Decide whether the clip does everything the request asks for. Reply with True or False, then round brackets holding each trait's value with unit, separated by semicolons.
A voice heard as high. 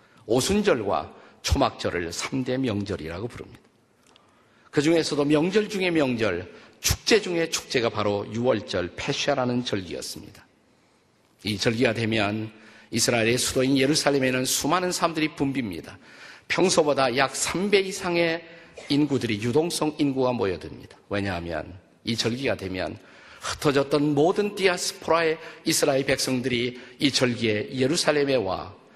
False (135 Hz)